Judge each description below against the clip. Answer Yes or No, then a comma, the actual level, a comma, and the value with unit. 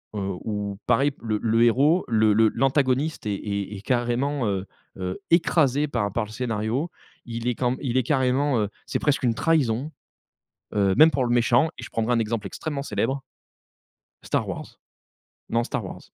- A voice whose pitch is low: Yes, low, 120 Hz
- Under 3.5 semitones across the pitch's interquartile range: No, average, 4.0 semitones